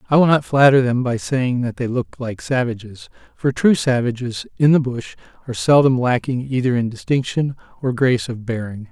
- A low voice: Yes, low, 125 Hz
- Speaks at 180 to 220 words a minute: Yes, average, 190 wpm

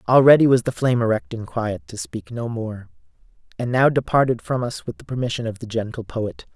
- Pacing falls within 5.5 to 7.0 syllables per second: Yes, 5.7 syllables/s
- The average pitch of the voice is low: Yes, low, 120 Hz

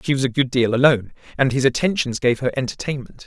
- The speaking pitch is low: Yes, low, 130 Hz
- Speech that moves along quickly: Yes, fast, 220 wpm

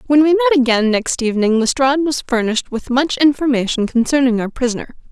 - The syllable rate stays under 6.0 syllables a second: No, 6.3 syllables/s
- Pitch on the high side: Yes, very high, 260 Hz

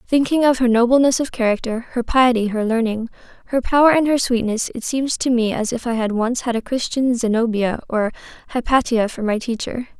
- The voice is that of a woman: Yes, female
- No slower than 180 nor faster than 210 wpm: Yes, average, 200 wpm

